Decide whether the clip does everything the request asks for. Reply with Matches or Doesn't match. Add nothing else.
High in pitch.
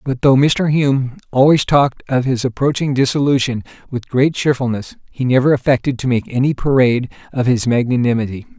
Doesn't match